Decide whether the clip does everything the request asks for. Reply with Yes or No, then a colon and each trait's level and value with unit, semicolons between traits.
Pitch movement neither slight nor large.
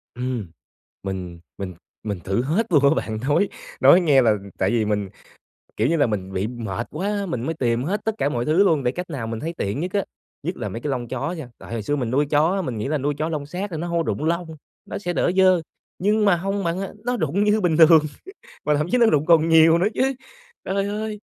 No: wide, 7.3 semitones